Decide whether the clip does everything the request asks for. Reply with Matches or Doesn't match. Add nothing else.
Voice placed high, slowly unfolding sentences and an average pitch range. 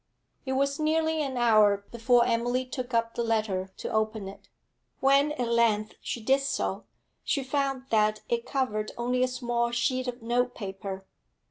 Doesn't match